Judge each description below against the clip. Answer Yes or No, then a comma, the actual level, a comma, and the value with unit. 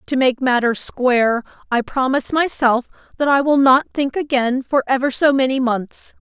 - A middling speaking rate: Yes, average, 170 wpm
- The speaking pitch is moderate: No, very high, 260 Hz